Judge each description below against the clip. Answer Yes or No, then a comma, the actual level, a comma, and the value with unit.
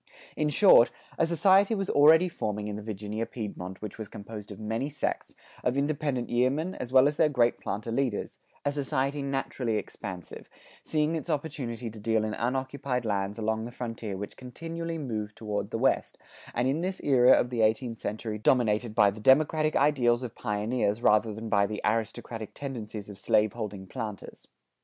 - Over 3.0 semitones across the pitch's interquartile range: Yes, average, 4.6 semitones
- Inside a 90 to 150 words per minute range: No, average, 175 wpm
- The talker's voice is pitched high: No, low, 120 Hz